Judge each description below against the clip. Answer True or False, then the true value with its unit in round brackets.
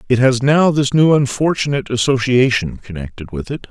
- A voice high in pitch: False (125 Hz)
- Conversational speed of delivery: True (160 wpm)